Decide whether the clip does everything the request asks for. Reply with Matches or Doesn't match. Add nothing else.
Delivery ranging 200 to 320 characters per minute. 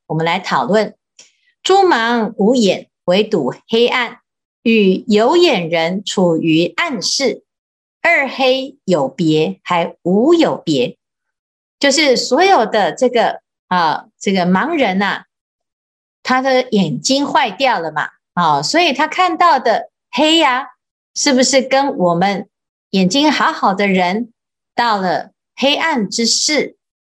Doesn't match